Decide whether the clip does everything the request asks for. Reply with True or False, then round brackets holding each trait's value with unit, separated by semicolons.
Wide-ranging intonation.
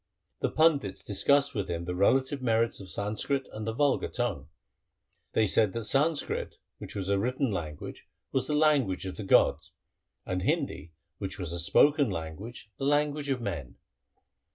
True (6.6 semitones)